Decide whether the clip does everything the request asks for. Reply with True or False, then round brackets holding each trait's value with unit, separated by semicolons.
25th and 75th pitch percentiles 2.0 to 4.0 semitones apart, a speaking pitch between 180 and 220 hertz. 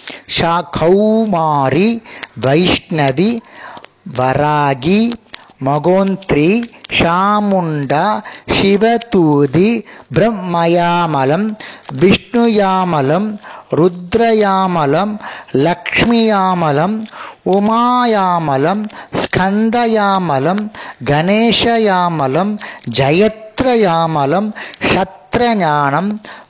False (5.4 semitones; 185 Hz)